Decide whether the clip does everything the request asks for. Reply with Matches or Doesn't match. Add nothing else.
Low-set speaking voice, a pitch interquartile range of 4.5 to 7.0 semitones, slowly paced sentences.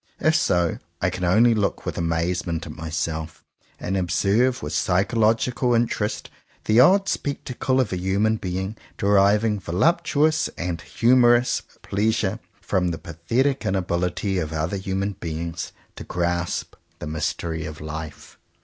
Matches